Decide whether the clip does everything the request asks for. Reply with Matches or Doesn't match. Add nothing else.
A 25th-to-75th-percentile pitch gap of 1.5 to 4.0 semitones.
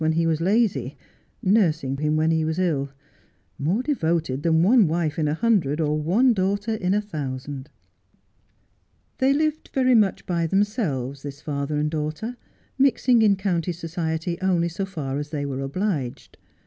Doesn't match